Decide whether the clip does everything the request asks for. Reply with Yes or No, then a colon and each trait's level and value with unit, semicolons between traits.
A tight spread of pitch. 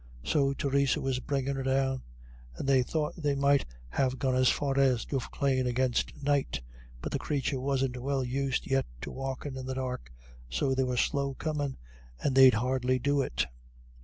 Yes: narrow, 1.3 semitones